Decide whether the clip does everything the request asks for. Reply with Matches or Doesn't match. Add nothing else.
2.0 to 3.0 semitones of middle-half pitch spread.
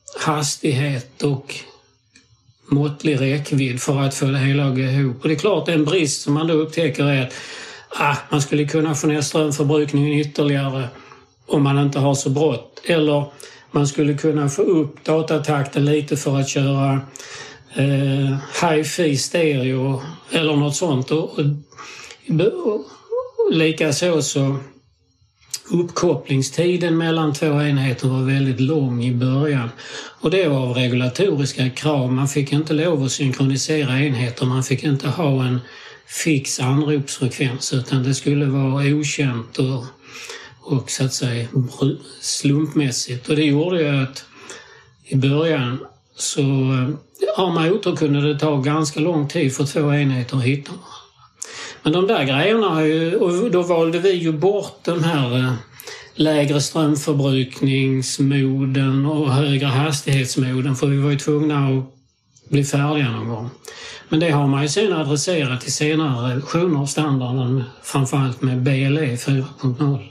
Matches